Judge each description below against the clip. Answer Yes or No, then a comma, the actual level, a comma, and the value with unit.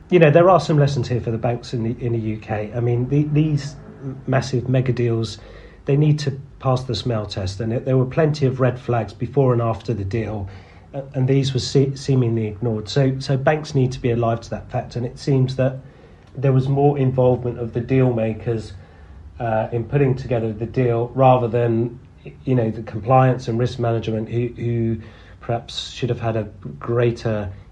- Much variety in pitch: No, average, 2.7 semitones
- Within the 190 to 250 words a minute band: Yes, average, 200 wpm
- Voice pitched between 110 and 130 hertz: Yes, low, 120 Hz